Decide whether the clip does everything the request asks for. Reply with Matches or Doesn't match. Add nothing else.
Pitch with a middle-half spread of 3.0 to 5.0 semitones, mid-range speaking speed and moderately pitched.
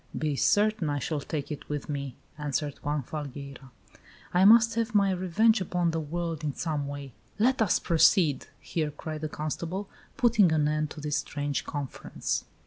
Matches